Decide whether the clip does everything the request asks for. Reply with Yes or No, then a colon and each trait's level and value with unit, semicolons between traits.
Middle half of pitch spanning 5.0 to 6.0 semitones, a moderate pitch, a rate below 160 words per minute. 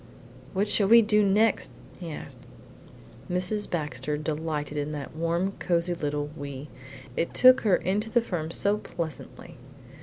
Yes: wide, 5.5 semitones; medium, 170 Hz; average, 145 wpm